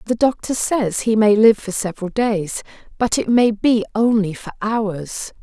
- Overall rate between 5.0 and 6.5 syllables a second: No, 4.3 syllables/s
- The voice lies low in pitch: No, high, 215 Hz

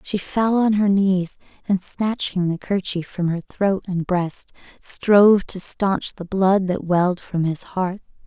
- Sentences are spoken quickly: No, average, 175 wpm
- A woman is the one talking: Yes, female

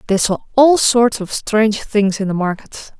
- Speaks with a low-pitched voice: No, high, 215 Hz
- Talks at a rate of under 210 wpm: Yes, average, 200 wpm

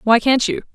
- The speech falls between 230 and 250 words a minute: Yes, fast, 240 wpm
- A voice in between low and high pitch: No, high, 245 Hz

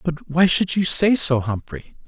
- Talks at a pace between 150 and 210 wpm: Yes, average, 200 wpm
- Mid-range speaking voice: Yes, medium, 160 Hz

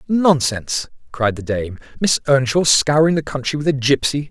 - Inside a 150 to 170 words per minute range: Yes, average, 165 wpm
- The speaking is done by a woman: No, male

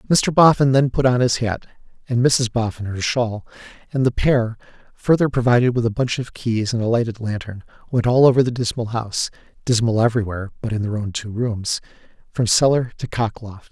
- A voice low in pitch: Yes, low, 120 Hz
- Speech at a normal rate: Yes, average, 190 wpm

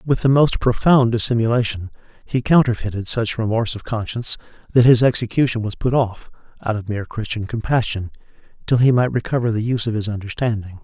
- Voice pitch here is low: Yes, low, 115 Hz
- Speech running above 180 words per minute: No, average, 170 wpm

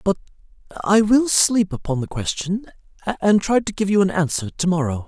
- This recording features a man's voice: Yes, male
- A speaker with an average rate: Yes, average, 190 wpm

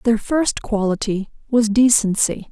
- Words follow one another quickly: No, slow, 120 wpm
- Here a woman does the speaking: Yes, female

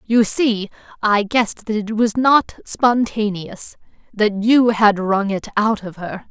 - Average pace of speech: Yes, average, 160 wpm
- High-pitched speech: Yes, high, 215 Hz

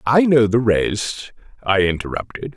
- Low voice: Yes, low, 110 Hz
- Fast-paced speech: No, average, 140 wpm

